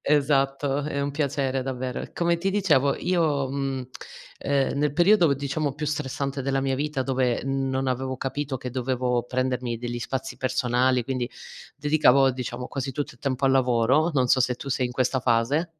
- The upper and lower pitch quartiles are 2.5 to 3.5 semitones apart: No, narrow, 1.9 semitones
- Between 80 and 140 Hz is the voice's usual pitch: Yes, low, 135 Hz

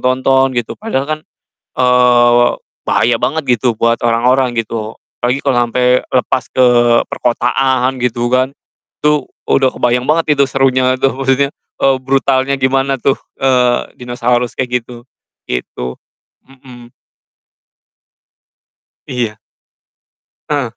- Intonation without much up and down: Yes, narrow, 1.7 semitones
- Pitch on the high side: No, low, 125 Hz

